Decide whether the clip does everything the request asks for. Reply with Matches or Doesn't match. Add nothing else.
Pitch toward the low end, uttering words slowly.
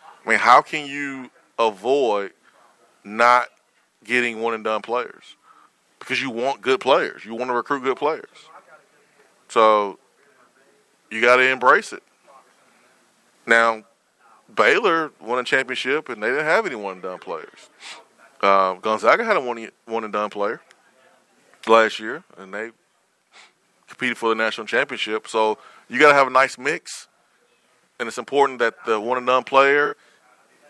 Doesn't match